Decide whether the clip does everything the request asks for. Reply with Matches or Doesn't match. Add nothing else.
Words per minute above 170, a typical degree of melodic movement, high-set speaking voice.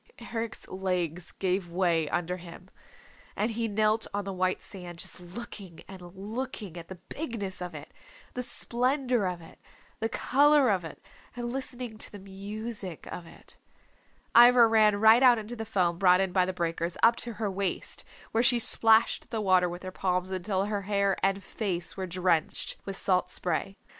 Matches